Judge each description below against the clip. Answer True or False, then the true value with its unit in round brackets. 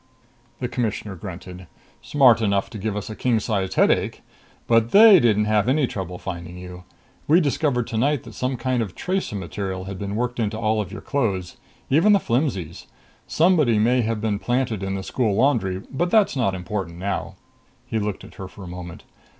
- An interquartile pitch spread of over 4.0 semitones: True (4.9 semitones)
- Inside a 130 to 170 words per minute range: False (185 wpm)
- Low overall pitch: True (110 Hz)